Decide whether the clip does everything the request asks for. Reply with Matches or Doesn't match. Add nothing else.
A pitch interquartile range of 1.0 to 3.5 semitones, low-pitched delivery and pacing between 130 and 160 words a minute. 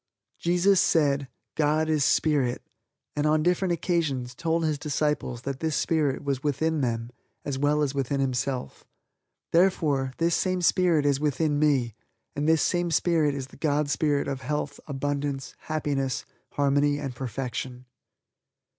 Doesn't match